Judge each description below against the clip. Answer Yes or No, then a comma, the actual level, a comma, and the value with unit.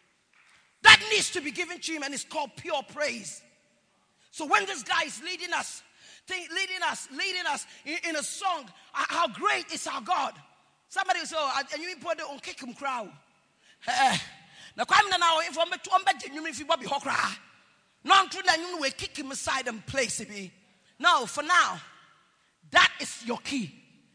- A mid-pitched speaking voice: No, very high, 325 Hz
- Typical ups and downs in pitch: Yes, average, 4.5 semitones